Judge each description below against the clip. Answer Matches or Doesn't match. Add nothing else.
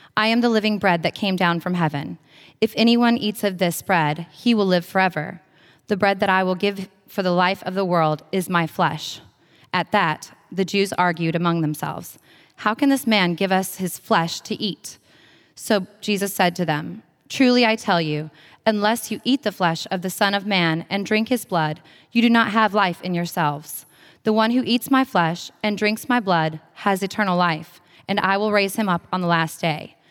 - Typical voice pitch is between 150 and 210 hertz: Matches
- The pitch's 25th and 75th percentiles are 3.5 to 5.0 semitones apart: Matches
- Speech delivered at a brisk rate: Matches